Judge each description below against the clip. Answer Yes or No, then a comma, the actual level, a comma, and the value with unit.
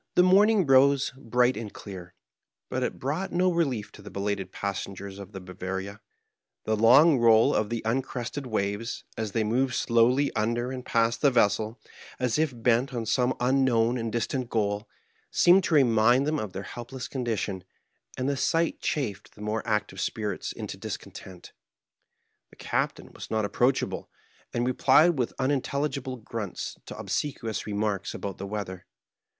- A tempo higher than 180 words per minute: No, average, 160 wpm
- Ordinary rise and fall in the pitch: Yes, average, 4.1 semitones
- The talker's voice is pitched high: No, low, 120 Hz